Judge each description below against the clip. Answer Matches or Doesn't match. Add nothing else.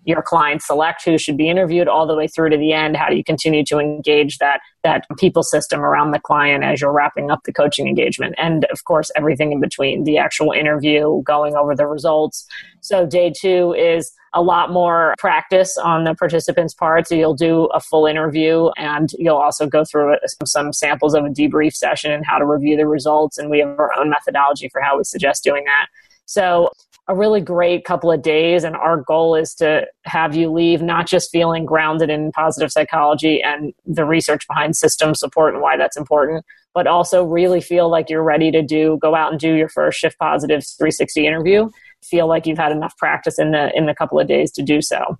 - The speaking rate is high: Matches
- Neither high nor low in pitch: Matches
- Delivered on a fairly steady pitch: Matches